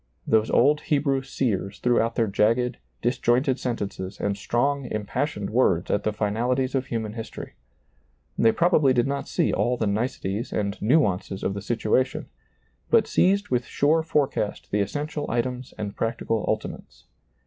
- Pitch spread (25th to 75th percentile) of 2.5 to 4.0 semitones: No, average, 4.4 semitones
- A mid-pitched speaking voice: No, low, 120 Hz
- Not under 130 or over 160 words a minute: Yes, average, 150 wpm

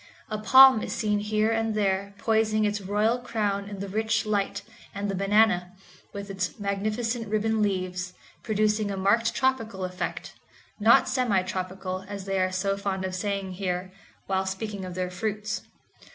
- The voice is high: Yes, high, 200 Hz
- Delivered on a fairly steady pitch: Yes, narrow, 2.3 semitones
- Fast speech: No, average, 160 wpm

